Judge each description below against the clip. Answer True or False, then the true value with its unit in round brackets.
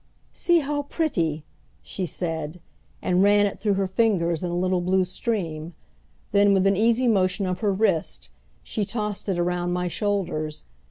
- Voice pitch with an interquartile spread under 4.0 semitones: True (3.0 semitones)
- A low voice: False (190 Hz)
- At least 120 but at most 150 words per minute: False (165 wpm)